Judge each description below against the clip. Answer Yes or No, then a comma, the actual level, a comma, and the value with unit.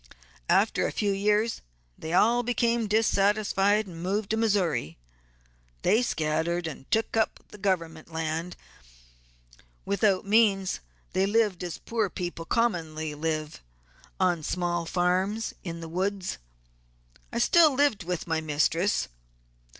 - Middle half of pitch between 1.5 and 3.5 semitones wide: No, average, 4.5 semitones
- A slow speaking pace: Yes, slow, 120 wpm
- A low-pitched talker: No, high, 190 Hz